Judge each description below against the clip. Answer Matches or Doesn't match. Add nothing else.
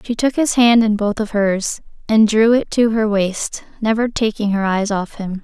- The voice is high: Matches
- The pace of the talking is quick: Matches